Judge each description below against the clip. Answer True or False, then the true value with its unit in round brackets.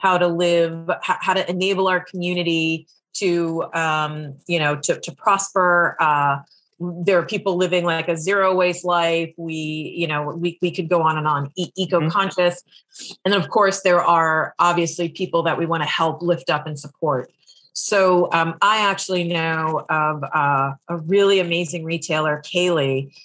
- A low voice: False (170 Hz)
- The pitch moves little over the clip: True (2.2 semitones)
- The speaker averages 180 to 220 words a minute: False (170 wpm)